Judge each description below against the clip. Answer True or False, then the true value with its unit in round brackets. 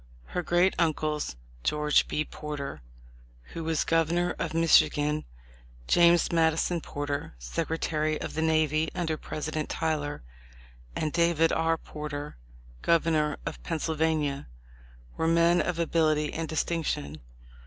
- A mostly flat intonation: True (1.6 semitones)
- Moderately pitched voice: True (160 Hz)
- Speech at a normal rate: False (120 wpm)